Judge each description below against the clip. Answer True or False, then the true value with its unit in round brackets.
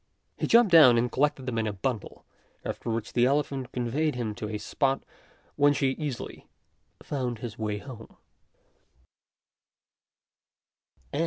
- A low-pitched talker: True (125 Hz)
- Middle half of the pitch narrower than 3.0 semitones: False (3.6 semitones)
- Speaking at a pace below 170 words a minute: True (135 wpm)